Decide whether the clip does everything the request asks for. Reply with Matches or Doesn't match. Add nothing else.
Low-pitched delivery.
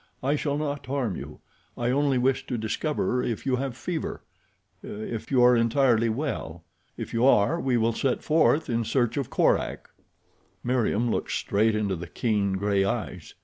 Matches